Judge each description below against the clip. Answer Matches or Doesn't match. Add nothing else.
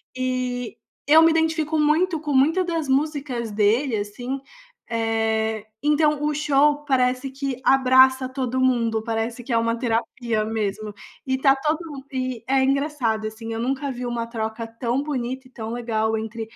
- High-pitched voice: Matches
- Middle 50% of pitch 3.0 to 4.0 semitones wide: Matches